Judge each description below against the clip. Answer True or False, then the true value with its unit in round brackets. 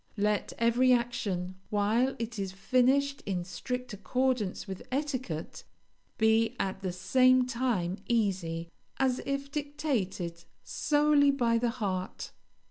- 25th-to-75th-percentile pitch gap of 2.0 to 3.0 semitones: False (5.2 semitones)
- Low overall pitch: False (230 Hz)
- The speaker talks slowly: True (120 wpm)